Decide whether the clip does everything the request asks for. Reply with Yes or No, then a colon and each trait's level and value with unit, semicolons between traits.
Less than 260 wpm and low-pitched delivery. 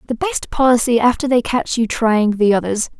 No: average, 200 wpm; high, 240 Hz